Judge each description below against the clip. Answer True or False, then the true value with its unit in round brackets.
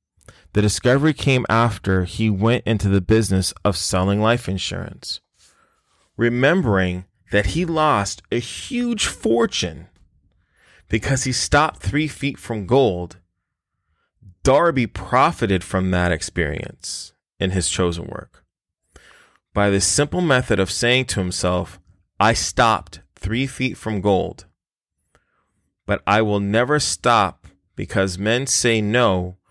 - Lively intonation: False (5.0 semitones)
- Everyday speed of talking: False (120 wpm)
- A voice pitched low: True (105 Hz)